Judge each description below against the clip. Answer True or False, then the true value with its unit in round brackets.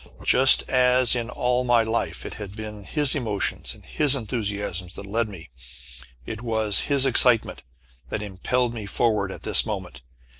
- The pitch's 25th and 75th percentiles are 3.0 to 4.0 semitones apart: True (3.4 semitones)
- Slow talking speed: False (160 wpm)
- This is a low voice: True (115 Hz)